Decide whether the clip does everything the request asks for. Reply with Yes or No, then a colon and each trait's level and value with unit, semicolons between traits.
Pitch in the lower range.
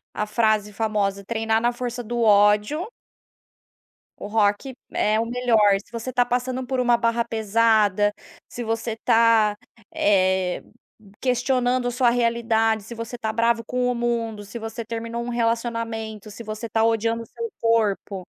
No: high, 230 Hz